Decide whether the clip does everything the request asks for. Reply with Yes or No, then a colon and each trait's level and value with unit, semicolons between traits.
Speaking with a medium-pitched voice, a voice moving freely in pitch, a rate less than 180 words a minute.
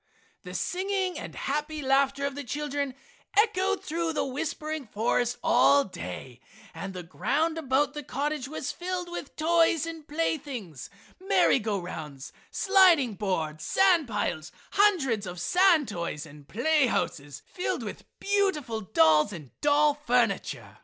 No: very high, 280 Hz; wide, 8.0 semitones; average, 140 wpm